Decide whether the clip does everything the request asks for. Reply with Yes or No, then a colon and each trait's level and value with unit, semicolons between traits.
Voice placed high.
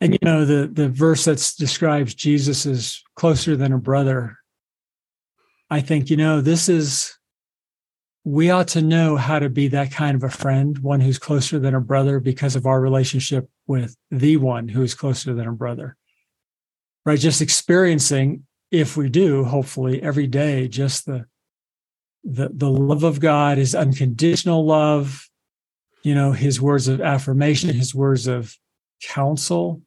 No: medium, 140 Hz